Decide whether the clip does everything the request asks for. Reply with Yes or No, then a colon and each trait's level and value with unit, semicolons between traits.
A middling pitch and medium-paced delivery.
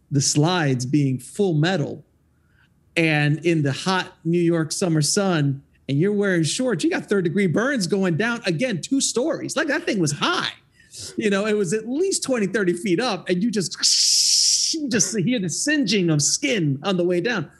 Yes: medium, 180 Hz; average, 190 wpm